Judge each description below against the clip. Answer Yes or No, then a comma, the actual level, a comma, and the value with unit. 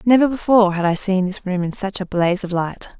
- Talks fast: Yes, fast, 260 wpm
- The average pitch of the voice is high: Yes, high, 195 Hz